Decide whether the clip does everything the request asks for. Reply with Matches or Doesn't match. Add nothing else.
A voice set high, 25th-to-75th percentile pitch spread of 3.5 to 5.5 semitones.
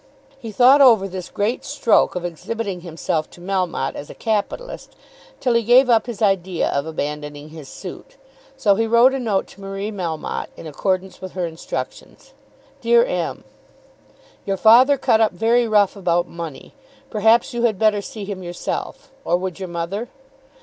Matches